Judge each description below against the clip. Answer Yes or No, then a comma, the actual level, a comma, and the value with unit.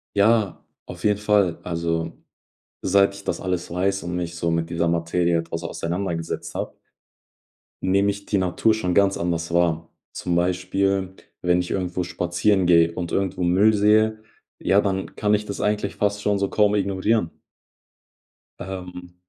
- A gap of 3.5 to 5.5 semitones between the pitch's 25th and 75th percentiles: No, narrow, 2.6 semitones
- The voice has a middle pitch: No, very low, 95 Hz